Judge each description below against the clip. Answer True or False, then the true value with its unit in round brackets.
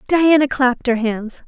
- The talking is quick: False (165 wpm)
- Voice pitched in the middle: False (260 Hz)